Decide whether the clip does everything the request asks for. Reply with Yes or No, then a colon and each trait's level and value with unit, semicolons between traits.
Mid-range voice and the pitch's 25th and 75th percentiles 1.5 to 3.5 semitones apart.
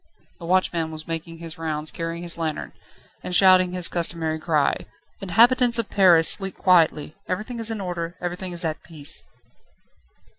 Yes: medium, 170 Hz; narrow, 2.4 semitones